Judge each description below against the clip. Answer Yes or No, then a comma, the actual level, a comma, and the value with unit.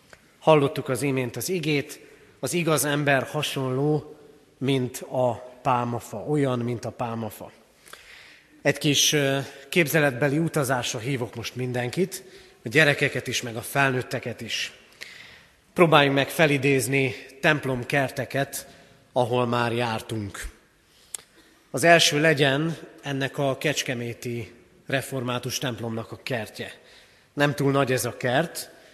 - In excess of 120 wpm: No, average, 110 wpm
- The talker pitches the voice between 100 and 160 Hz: Yes, low, 135 Hz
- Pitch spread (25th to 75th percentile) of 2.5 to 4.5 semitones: Yes, average, 2.8 semitones